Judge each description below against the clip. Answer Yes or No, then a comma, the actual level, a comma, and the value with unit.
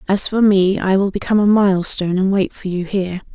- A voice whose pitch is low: No, high, 195 Hz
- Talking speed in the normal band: No, fast, 235 wpm